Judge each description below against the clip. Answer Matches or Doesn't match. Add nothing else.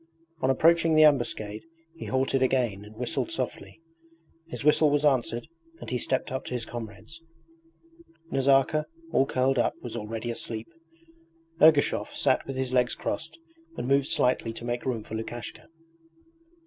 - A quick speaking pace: Doesn't match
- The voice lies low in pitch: Matches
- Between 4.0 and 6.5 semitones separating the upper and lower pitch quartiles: Doesn't match